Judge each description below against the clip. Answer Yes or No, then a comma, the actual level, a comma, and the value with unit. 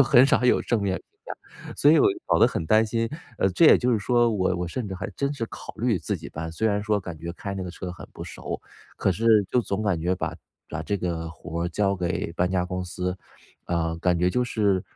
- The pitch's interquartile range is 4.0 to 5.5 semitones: Yes, average, 4.3 semitones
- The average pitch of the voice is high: No, very low, 95 Hz